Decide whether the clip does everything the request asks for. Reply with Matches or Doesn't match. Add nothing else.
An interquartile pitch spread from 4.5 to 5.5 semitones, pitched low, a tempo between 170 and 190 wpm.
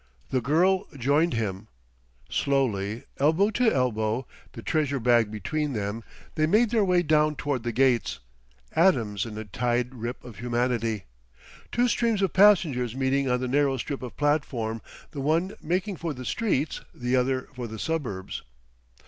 Doesn't match